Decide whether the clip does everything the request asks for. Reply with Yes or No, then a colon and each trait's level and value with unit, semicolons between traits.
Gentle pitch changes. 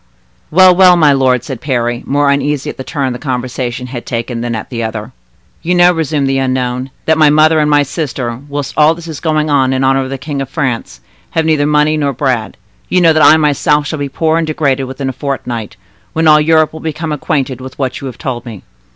No: average, 3.2 semitones